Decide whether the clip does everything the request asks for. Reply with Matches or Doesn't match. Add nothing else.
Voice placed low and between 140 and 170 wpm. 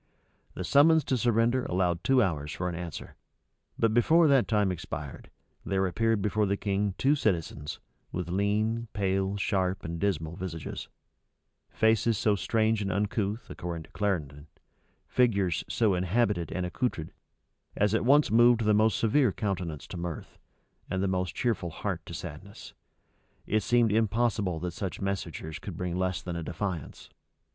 Matches